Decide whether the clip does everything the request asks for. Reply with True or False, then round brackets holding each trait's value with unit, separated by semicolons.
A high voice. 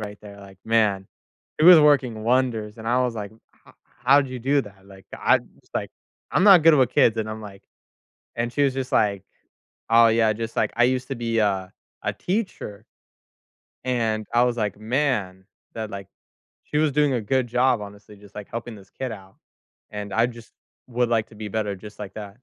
False (115 Hz)